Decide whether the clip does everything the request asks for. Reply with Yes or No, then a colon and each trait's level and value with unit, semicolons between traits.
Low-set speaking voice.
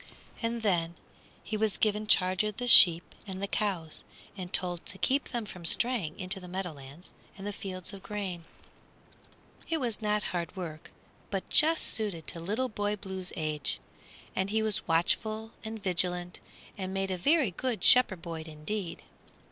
No: high, 190 Hz